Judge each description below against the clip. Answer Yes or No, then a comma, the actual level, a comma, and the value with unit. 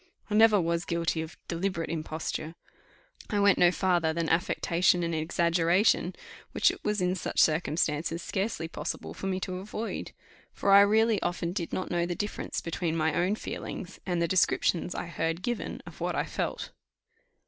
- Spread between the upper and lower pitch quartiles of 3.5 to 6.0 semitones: No, average, 2.7 semitones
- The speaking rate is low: No, average, 170 wpm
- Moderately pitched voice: Yes, medium, 175 Hz